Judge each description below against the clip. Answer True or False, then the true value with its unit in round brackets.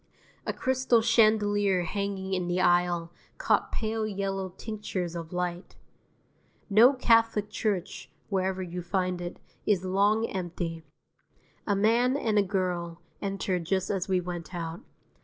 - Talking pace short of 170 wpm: True (135 wpm)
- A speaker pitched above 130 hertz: True (190 Hz)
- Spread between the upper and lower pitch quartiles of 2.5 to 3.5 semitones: True (3.1 semitones)